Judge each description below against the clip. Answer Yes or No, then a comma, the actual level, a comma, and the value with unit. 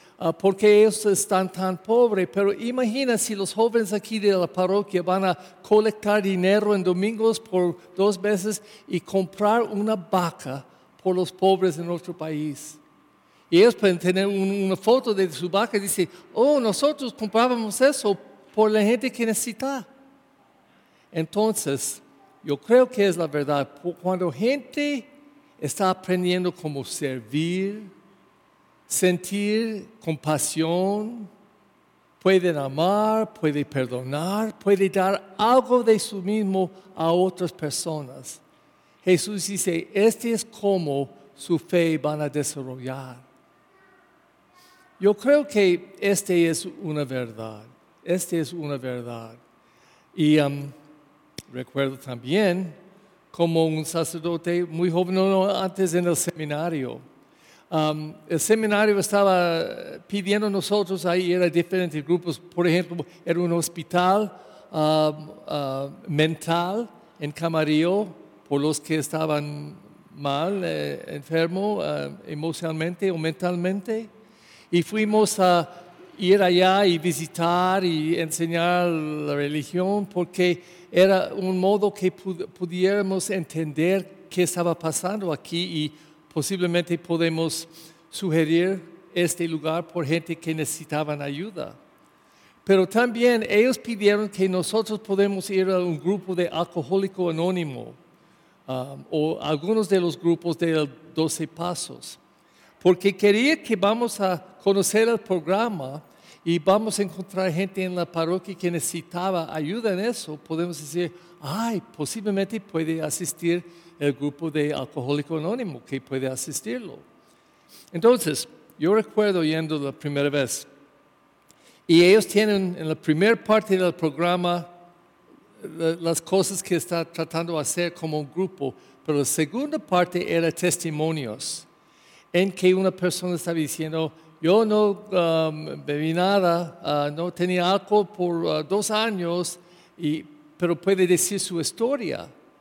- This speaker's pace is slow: Yes, slow, 125 wpm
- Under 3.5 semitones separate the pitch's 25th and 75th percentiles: No, average, 3.8 semitones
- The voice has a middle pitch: Yes, medium, 180 Hz